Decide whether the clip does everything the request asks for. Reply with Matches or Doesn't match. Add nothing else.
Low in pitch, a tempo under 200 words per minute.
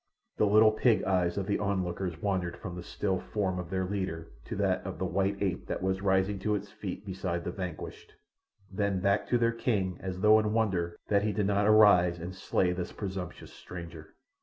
Doesn't match